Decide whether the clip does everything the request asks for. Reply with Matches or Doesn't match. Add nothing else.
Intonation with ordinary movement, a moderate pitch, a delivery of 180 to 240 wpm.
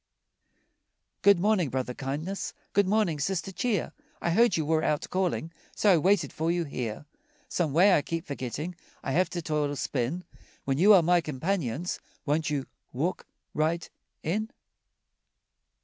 Doesn't match